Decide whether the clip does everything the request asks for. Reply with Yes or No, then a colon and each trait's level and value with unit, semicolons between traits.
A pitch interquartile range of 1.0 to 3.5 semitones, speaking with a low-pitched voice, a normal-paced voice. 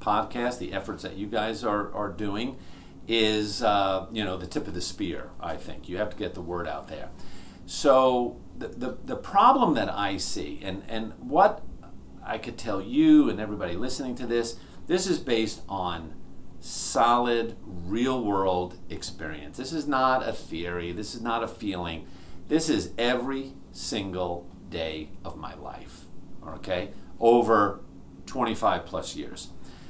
No: average, 4.5 semitones; low, 100 Hz; average, 160 wpm